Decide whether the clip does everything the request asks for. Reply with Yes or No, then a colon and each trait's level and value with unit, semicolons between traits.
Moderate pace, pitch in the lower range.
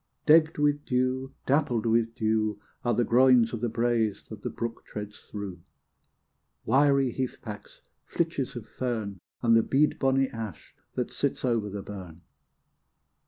Yes: average, 150 wpm; low, 115 Hz